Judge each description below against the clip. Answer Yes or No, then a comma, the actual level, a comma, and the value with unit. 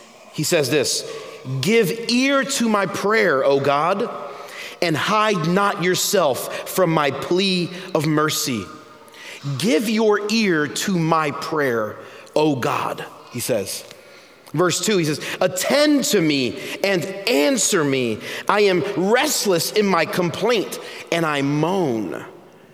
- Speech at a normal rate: No, slow, 125 wpm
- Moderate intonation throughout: No, wide, 6.2 semitones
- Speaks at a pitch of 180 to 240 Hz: Yes, medium, 185 Hz